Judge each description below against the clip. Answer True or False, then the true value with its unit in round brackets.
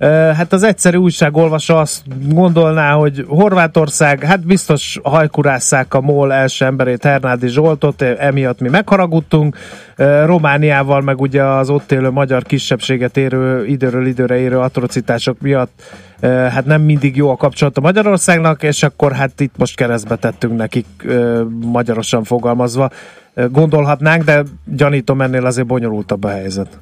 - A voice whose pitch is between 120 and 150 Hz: True (140 Hz)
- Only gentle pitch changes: False (3.4 semitones)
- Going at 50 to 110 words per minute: False (135 wpm)